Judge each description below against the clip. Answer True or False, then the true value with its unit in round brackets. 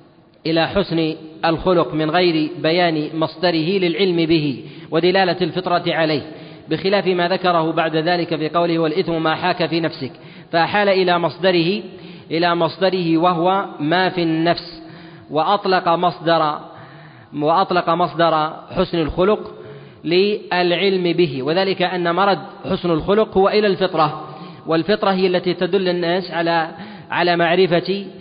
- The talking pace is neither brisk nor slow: True (120 wpm)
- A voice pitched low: False (170 Hz)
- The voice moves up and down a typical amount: False (2.2 semitones)